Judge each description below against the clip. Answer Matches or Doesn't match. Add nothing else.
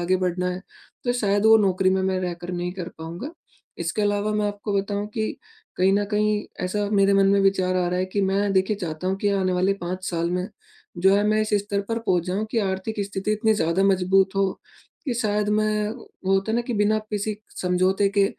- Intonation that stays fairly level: Matches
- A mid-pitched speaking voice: Doesn't match